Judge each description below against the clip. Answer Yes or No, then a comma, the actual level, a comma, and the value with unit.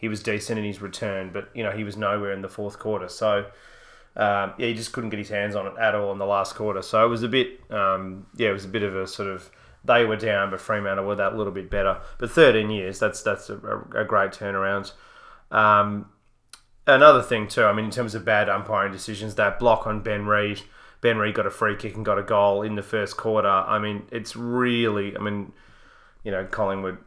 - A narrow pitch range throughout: Yes, narrow, 1.8 semitones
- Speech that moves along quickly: Yes, fast, 235 wpm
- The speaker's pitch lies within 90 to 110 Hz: Yes, low, 105 Hz